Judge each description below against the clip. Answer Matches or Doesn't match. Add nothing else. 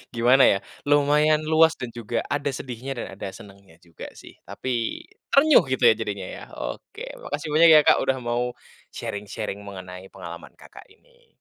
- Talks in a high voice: Doesn't match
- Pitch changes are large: Matches